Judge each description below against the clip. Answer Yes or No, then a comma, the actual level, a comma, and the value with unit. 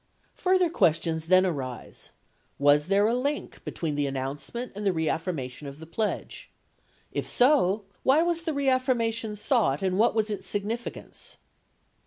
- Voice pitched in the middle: No, high, 200 Hz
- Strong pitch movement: Yes, wide, 7.7 semitones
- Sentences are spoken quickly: No, average, 150 wpm